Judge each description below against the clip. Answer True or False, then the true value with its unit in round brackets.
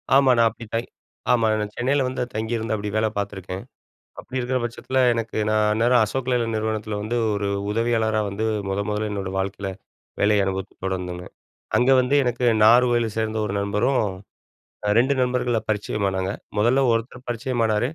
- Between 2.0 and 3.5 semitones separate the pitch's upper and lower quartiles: True (2.9 semitones)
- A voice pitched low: True (110 Hz)